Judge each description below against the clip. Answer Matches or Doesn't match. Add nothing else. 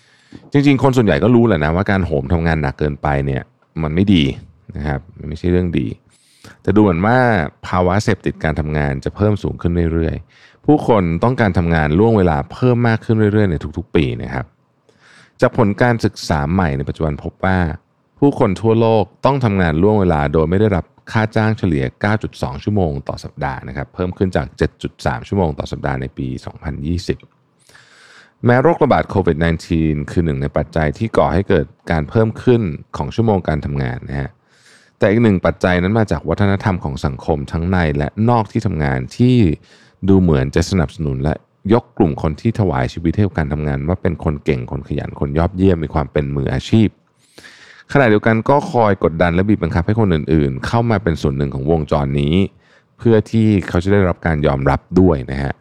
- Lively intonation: Matches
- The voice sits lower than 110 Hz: Matches